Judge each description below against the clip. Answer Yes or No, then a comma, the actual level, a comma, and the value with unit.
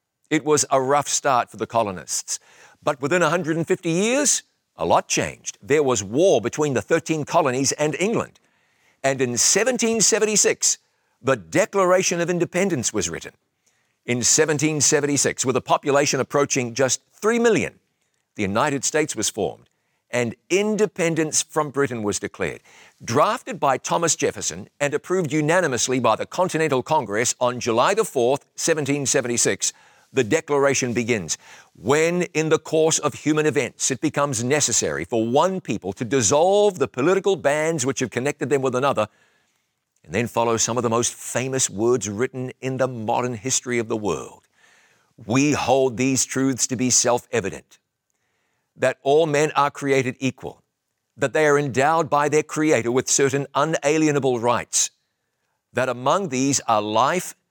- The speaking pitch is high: No, medium, 140 Hz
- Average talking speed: Yes, average, 150 wpm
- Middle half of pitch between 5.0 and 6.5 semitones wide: No, average, 4.2 semitones